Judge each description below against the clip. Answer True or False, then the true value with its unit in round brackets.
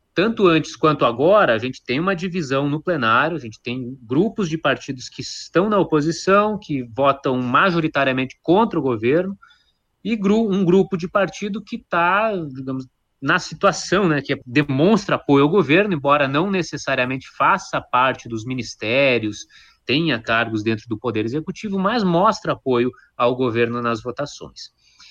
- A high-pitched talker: False (150 Hz)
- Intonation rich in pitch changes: True (6.8 semitones)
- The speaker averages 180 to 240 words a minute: False (155 wpm)